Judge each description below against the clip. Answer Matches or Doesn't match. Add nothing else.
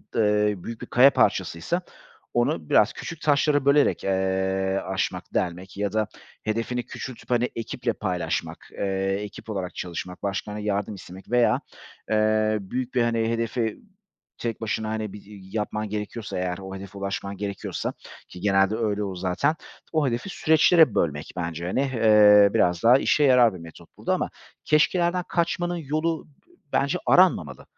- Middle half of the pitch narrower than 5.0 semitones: Matches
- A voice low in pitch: Matches